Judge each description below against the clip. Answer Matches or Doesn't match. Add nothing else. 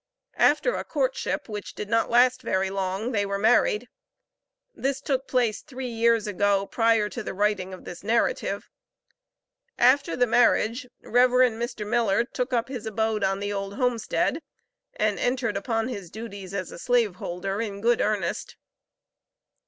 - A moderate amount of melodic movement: Matches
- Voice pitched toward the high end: Matches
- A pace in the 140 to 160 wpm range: Matches